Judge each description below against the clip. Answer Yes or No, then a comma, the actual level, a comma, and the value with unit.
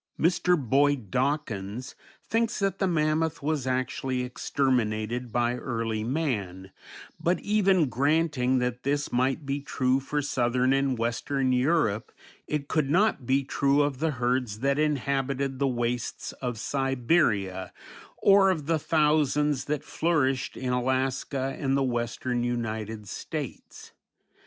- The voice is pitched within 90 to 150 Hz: Yes, low, 135 Hz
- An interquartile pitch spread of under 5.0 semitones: Yes, average, 3.4 semitones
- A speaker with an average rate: No, slow, 130 wpm